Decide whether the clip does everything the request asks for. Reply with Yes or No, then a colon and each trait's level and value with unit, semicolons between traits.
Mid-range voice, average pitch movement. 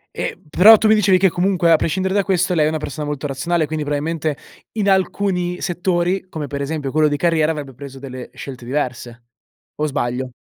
Yes: medium, 155 Hz; average, 4.2 semitones